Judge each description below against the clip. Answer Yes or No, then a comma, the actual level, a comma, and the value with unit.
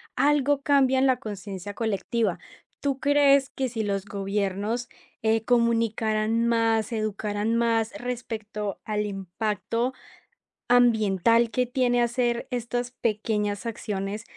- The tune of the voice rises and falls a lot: No, average, 2.8 semitones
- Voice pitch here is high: Yes, high, 225 Hz